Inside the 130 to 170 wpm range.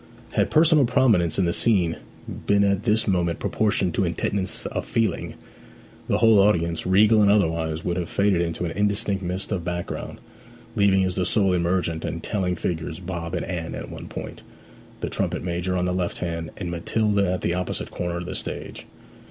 No: average, 185 wpm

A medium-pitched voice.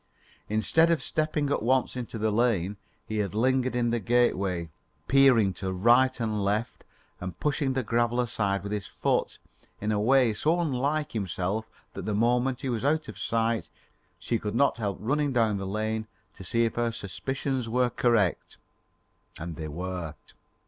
No: low, 115 Hz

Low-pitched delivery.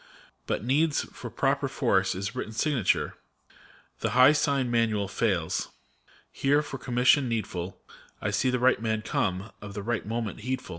Yes: low, 115 Hz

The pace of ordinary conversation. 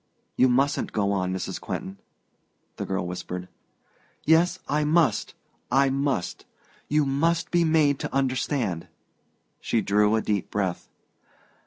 No: slow, 130 wpm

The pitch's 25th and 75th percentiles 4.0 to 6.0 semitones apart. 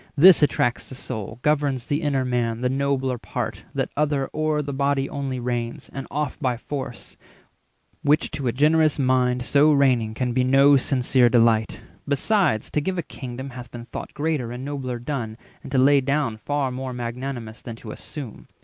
No: average, 2.8 semitones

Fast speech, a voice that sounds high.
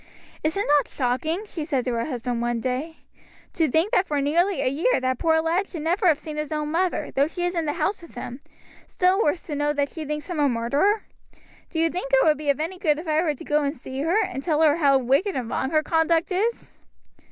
Yes: fast, 255 wpm; very high, 310 Hz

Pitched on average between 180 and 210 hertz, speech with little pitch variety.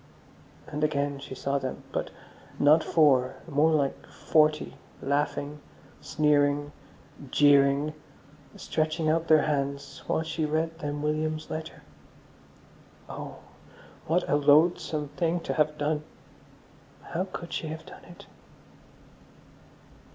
No: medium, 150 Hz; narrow, 1.7 semitones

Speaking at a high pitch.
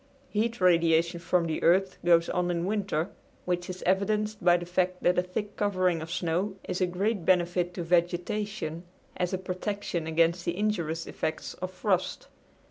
No: medium, 180 Hz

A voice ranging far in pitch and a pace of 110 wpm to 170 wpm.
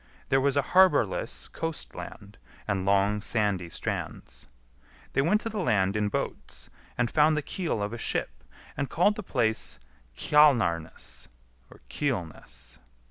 Yes: wide, 7.0 semitones; average, 140 wpm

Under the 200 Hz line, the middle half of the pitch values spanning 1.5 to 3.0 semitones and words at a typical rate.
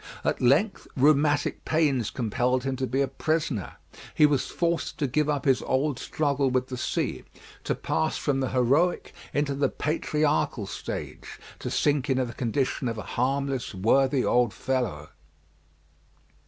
Yes: low, 135 Hz; average, 2.7 semitones; average, 155 wpm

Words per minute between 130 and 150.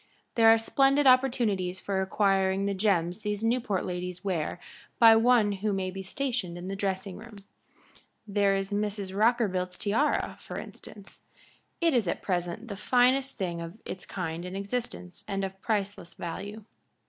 No: average, 160 wpm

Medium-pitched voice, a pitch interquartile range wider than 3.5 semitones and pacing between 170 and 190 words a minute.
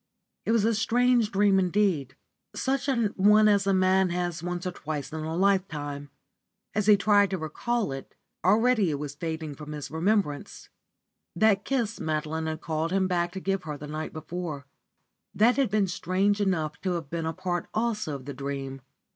Yes: medium, 180 Hz; average, 4.8 semitones; average, 185 wpm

